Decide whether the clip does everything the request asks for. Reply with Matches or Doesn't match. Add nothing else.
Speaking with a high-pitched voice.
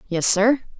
Matches